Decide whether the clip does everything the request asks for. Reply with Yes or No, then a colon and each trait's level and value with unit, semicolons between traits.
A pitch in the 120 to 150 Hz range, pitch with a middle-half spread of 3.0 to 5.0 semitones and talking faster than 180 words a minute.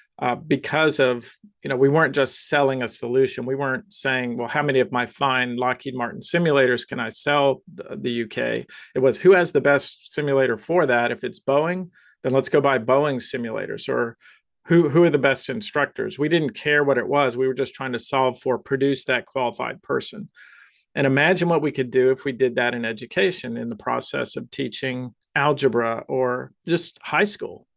Yes: low, 135 Hz; average, 3.6 semitones; average, 200 wpm